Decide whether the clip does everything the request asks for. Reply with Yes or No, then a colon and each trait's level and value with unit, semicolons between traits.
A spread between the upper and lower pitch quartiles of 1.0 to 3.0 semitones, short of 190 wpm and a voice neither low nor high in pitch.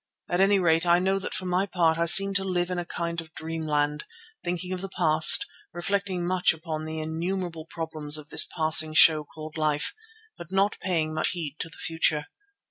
No: narrow, 2.5 semitones; average, 200 wpm; medium, 165 Hz